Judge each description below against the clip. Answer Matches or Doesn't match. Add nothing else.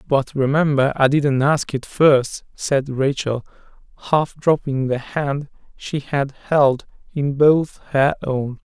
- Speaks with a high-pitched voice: Doesn't match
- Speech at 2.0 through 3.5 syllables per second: Matches